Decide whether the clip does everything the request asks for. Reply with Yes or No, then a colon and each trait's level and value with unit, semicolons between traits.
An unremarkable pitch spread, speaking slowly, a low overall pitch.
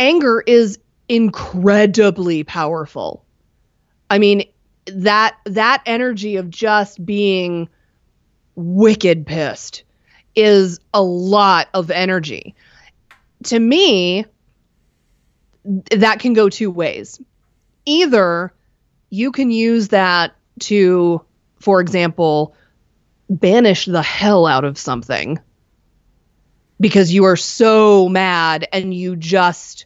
No: average, 3.6 semitones; slow, 95 wpm; high, 195 Hz